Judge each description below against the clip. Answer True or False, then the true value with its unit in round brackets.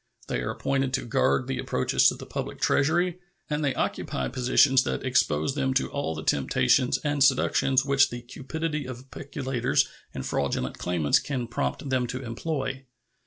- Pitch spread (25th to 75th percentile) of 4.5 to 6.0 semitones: False (2.5 semitones)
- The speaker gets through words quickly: False (165 wpm)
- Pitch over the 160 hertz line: False (130 Hz)